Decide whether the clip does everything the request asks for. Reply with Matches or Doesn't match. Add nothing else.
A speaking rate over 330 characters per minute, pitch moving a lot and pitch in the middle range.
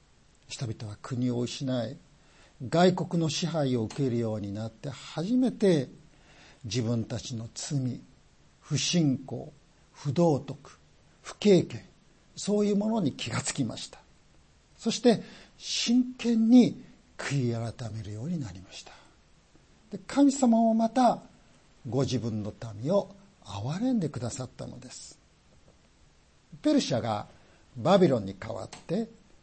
Doesn't match